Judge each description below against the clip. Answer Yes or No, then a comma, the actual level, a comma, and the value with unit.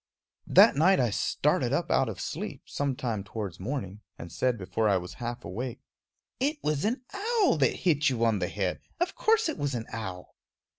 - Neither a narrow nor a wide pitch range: No, wide, 8.1 semitones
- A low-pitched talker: Yes, low, 125 Hz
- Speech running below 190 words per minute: No, average, 195 wpm